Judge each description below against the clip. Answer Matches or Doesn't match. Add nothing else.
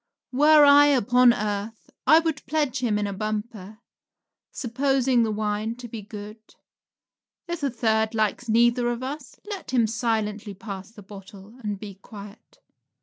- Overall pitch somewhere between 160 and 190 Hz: Doesn't match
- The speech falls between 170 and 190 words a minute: Doesn't match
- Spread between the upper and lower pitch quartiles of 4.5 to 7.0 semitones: Doesn't match